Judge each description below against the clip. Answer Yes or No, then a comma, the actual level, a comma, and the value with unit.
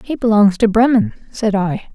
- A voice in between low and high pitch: No, high, 220 Hz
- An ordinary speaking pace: Yes, average, 185 wpm